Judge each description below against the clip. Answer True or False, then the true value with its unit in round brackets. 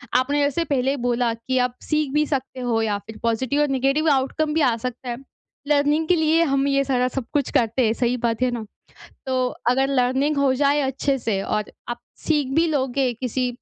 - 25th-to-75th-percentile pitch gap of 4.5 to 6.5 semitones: False (2.7 semitones)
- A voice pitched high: True (265 Hz)